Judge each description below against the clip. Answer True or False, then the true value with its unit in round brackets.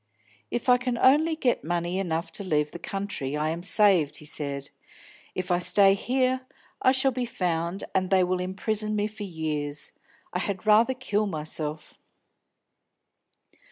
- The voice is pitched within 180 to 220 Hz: True (190 Hz)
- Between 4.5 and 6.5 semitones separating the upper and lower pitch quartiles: True (5.1 semitones)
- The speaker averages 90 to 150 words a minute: False (160 wpm)